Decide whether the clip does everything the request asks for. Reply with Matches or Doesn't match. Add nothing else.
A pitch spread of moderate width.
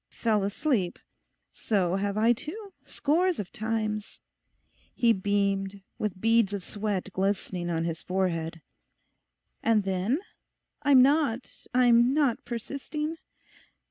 Matches